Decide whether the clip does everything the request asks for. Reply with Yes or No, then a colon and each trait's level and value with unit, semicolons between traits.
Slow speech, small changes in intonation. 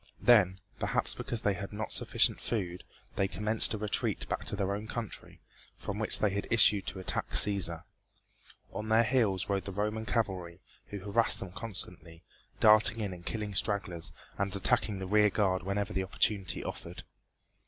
No: average, 170 wpm; narrow, 2.3 semitones